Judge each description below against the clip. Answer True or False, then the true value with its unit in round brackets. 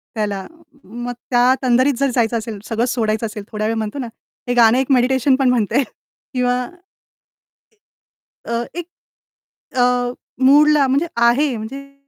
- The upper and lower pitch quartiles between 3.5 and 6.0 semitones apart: False (2.8 semitones)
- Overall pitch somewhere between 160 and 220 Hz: False (245 Hz)